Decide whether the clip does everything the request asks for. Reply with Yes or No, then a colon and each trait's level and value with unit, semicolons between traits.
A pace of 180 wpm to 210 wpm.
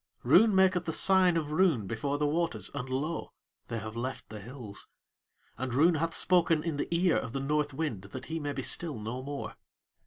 Yes: fast, 205 wpm